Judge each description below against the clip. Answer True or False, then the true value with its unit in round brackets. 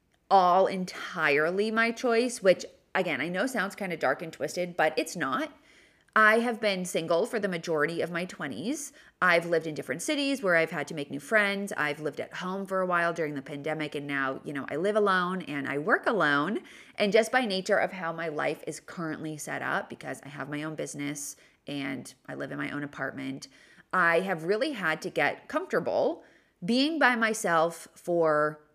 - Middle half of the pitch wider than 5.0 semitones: True (5.5 semitones)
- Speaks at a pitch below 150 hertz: False (170 Hz)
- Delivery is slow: False (200 wpm)